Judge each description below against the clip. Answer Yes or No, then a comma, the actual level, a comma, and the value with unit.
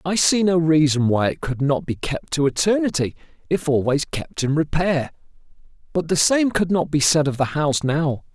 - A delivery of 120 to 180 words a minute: No, average, 200 wpm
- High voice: No, medium, 155 Hz